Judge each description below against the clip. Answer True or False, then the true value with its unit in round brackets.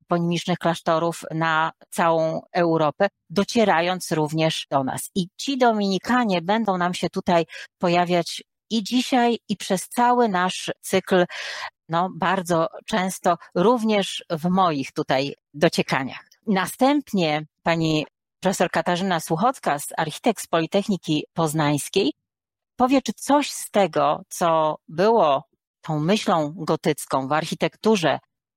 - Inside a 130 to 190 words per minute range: False (110 wpm)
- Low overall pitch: False (180 Hz)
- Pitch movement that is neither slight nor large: True (4.1 semitones)